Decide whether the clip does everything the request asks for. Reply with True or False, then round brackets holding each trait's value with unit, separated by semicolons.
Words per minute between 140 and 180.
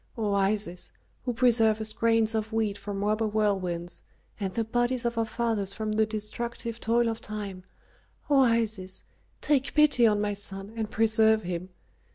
True (160 wpm)